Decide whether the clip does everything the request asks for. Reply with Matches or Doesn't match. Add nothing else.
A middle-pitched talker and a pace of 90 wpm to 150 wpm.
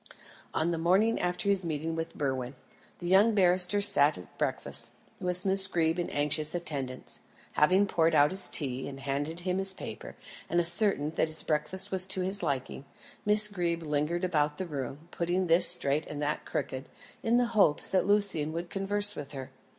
Doesn't match